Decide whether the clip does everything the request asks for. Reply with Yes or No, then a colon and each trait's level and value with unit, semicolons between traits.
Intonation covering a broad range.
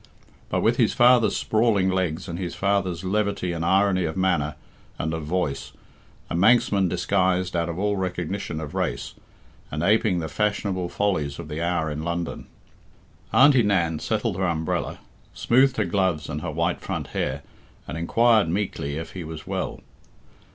No: average, 3.7 semitones